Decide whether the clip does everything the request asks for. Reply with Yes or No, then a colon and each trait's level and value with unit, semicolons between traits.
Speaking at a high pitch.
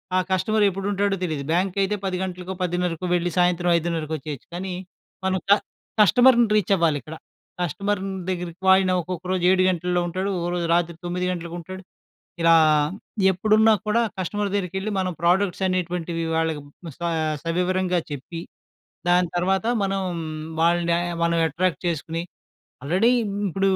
No: medium, 180 Hz